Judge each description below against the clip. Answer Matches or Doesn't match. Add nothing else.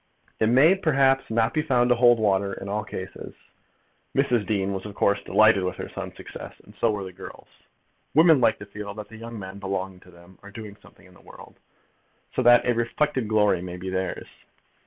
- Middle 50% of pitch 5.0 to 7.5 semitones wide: Doesn't match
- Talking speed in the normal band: Doesn't match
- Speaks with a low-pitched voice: Matches